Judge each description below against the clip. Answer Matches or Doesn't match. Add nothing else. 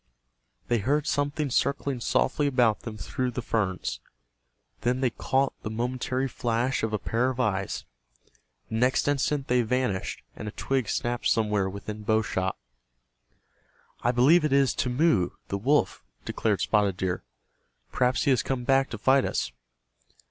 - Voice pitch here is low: Matches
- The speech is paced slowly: Doesn't match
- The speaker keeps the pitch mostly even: Doesn't match